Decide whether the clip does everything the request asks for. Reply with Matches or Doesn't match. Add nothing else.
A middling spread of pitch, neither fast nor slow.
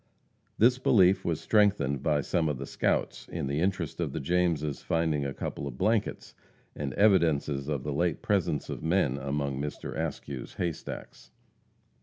Matches